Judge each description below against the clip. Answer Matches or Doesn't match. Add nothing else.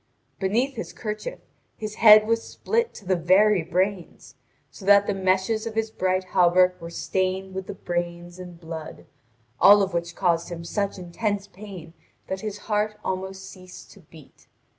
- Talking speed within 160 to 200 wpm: Matches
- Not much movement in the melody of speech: Doesn't match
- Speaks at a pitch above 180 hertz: Matches